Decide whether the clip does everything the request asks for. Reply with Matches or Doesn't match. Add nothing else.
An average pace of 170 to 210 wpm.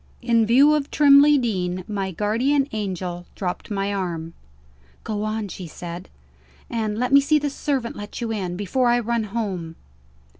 Doesn't match